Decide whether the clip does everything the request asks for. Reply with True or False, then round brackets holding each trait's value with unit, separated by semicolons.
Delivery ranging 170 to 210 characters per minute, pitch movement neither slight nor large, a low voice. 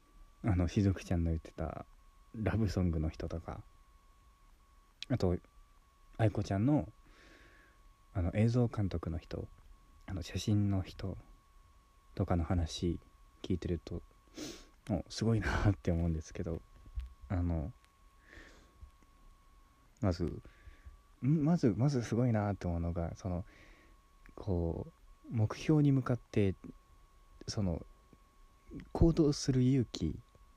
True (200 characters per minute; 4.7 semitones; 90 Hz)